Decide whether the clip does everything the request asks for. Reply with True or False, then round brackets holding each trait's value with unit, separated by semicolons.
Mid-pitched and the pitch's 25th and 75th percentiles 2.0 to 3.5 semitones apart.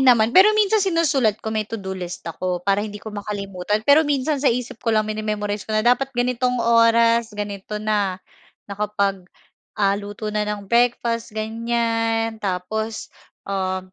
False (215 Hz; 2.5 semitones)